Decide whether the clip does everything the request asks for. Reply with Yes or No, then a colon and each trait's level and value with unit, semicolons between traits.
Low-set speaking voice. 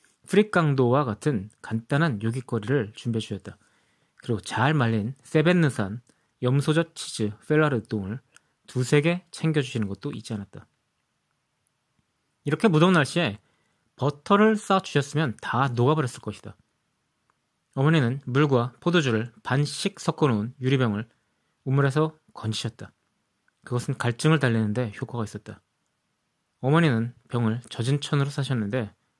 Yes: low, 130 Hz